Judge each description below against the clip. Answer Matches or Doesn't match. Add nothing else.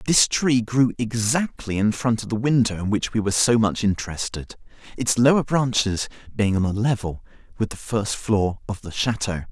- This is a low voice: Matches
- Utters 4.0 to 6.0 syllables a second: Matches